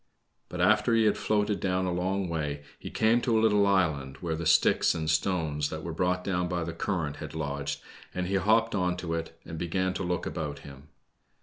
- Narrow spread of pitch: No, average, 3.6 semitones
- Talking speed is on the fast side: Yes, fast, 215 wpm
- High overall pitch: No, very low, 90 Hz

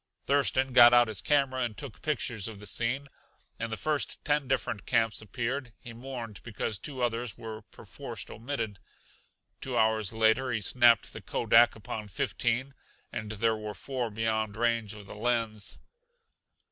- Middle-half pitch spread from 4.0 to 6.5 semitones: No, average, 2.7 semitones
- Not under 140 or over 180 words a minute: Yes, average, 160 wpm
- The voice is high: No, low, 115 Hz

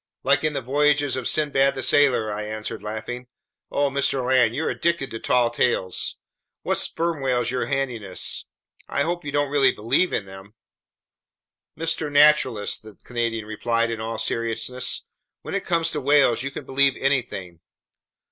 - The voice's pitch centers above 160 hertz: No, low, 130 Hz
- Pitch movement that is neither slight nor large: Yes, average, 4.1 semitones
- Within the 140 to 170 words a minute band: Yes, average, 165 wpm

